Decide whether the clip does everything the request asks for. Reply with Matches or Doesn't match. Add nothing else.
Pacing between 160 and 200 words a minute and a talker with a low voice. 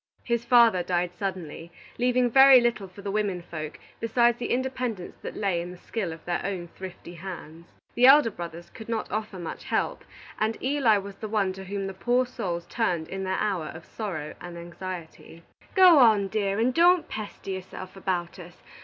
Doesn't match